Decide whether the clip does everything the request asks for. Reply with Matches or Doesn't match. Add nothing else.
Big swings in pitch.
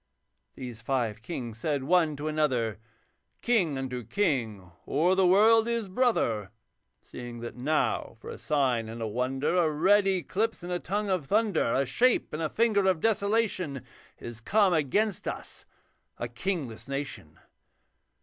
Matches